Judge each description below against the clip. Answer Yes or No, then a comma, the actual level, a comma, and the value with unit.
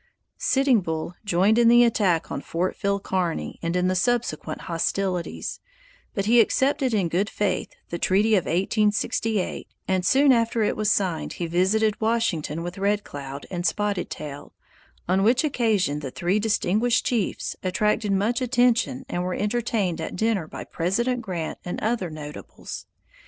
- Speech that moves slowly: No, average, 155 wpm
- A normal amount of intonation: Yes, average, 4.4 semitones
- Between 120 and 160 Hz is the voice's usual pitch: No, high, 200 Hz